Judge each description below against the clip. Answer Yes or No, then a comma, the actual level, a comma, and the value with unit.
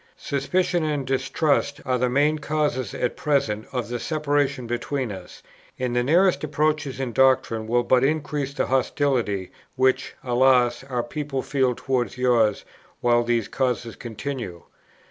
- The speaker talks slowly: No, average, 145 wpm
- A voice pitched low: Yes, low, 130 Hz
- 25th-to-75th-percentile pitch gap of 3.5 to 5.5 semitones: No, average, 3.0 semitones